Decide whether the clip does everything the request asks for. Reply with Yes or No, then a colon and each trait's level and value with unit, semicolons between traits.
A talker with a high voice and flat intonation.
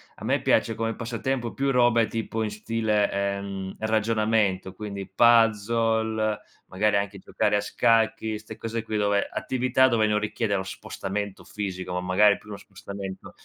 No: low, 105 Hz; narrow, 2.2 semitones